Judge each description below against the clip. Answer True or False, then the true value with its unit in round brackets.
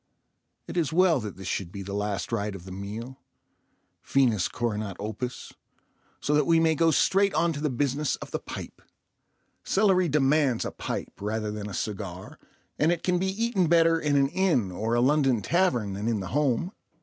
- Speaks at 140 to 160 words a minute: False (185 wpm)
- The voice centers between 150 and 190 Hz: False (130 Hz)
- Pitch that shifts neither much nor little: False (7.7 semitones)